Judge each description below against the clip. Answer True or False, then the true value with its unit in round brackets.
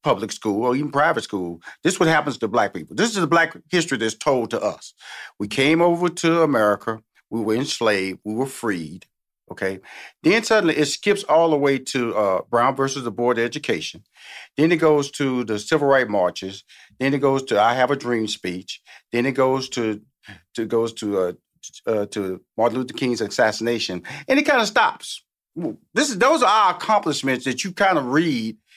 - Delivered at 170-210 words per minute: True (200 wpm)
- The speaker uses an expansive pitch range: True (6.5 semitones)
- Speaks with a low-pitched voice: True (130 Hz)